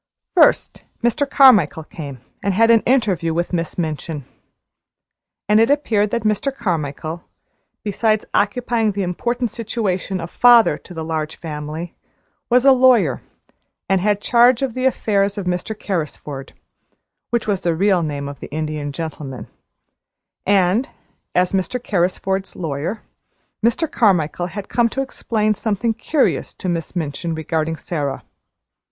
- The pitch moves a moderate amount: No, wide, 5.9 semitones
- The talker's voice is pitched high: Yes, high, 195 Hz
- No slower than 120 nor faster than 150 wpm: Yes, average, 140 wpm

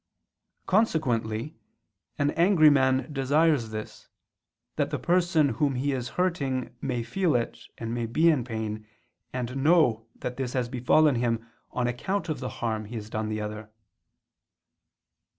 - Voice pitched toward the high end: No, low, 130 Hz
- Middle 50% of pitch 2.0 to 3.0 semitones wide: No, average, 5.0 semitones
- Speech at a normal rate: Yes, average, 145 wpm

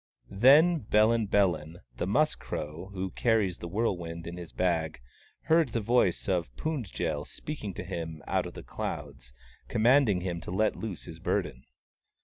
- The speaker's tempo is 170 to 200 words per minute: No, average, 160 wpm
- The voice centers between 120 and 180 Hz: No, very low, 95 Hz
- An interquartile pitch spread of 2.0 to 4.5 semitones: No, average, 5.3 semitones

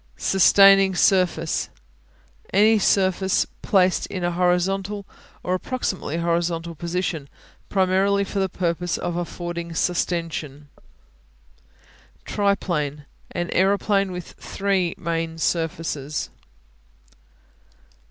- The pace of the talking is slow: Yes, slow, 85 wpm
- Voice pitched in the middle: Yes, medium, 180 Hz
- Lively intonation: No, narrow, 2.5 semitones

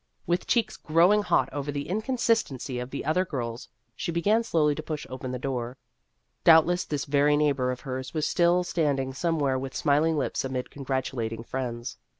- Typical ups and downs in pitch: Yes, average, 4.3 semitones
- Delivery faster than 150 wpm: Yes, average, 170 wpm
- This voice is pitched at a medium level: Yes, medium, 145 Hz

